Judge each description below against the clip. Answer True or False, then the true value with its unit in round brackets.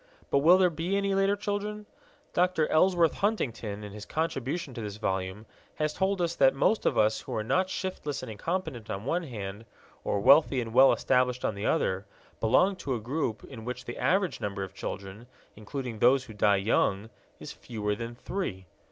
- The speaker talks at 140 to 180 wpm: False (190 wpm)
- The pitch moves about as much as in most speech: False (8.5 semitones)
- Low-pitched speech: True (130 Hz)